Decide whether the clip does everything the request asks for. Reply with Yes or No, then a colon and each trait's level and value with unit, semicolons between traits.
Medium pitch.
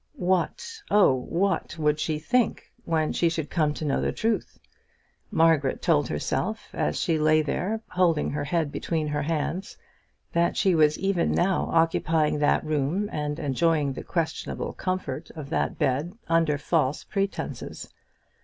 Yes: medium, 160 Hz